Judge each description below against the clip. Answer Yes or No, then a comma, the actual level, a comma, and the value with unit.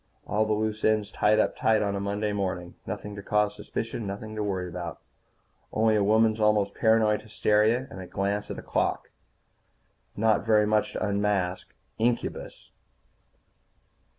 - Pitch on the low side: Yes, low, 105 Hz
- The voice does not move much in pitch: Yes, narrow, 1.4 semitones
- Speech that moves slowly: No, average, 155 wpm